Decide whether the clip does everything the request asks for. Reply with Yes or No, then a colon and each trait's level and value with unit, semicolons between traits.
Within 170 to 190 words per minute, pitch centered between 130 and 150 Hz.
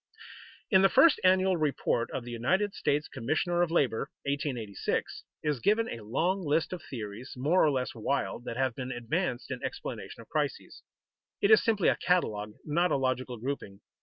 Yes: average, 180 wpm; medium, 140 Hz